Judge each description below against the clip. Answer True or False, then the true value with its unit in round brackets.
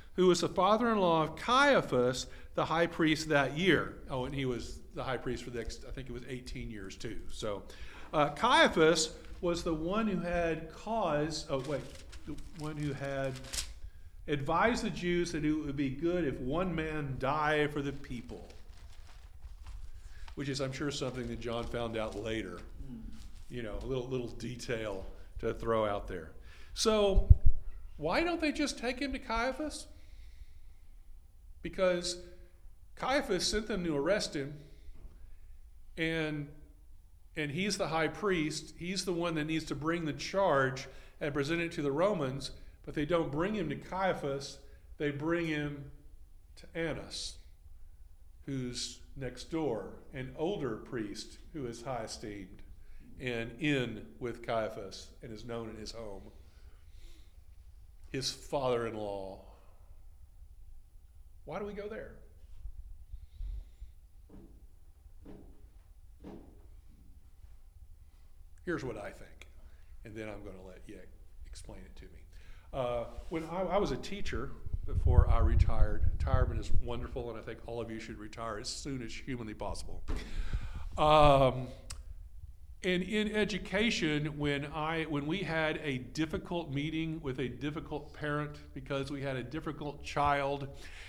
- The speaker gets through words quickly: False (140 wpm)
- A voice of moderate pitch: False (125 Hz)